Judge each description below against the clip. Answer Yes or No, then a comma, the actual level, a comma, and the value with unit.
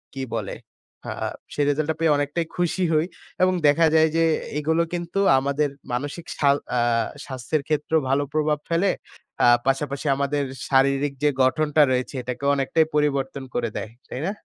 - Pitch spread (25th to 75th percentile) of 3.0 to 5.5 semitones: No, narrow, 2.5 semitones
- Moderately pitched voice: Yes, medium, 145 Hz